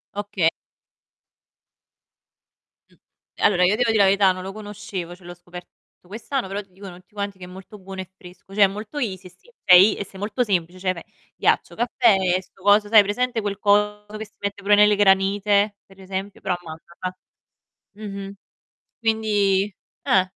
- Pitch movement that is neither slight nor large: No, narrow, 1.9 semitones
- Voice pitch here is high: Yes, high, 200 Hz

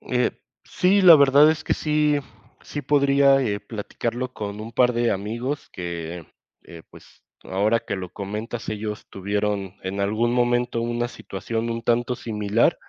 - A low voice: Yes, low, 115 Hz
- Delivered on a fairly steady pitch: No, average, 3.8 semitones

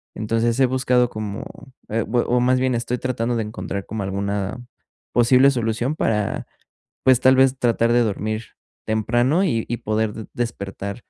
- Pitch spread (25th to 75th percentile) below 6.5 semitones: Yes, average, 2.7 semitones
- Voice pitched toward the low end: Yes, low, 115 Hz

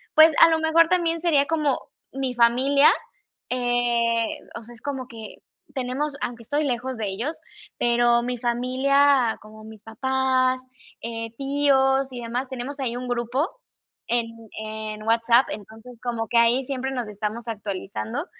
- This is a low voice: No, high, 245 Hz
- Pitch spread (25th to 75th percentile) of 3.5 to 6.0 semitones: No, average, 2.7 semitones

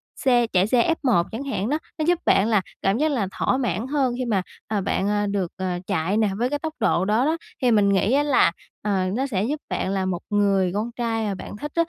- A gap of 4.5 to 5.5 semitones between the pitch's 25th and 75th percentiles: Yes, average, 5.0 semitones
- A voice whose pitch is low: No, high, 220 Hz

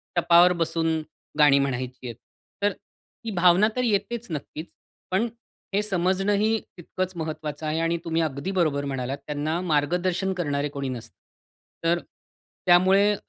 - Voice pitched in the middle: Yes, medium, 170 Hz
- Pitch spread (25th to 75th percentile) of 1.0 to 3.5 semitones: No, average, 4.2 semitones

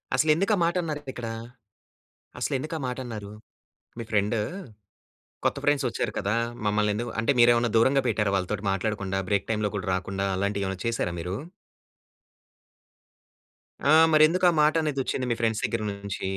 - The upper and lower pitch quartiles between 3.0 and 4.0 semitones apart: No, average, 5.1 semitones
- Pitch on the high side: No, low, 115 Hz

